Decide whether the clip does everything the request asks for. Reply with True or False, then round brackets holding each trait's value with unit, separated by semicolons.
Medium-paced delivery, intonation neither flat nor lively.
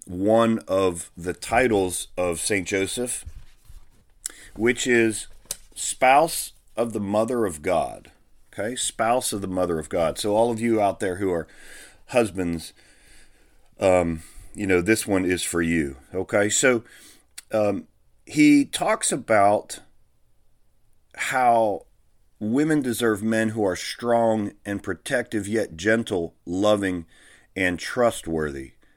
False (120 wpm; 4.0 semitones)